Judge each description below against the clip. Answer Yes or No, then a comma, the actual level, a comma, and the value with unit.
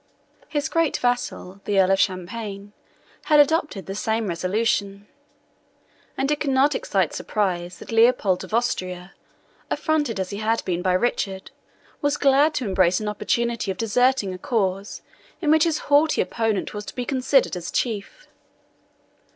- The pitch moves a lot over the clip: Yes, wide, 5.7 semitones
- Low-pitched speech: No, high, 220 Hz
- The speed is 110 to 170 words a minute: Yes, average, 155 wpm